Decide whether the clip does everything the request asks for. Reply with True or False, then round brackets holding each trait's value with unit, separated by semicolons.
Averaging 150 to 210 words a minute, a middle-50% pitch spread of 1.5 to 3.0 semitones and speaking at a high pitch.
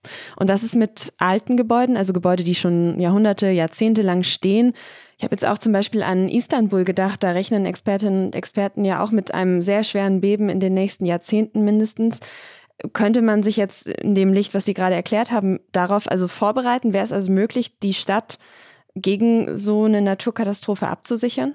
True (185 wpm; 2.6 semitones; 205 Hz)